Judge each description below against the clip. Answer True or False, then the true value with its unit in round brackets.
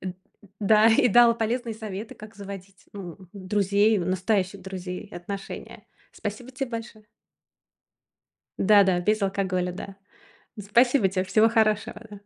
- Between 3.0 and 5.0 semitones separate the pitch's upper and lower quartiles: False (2.6 semitones)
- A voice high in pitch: True (205 Hz)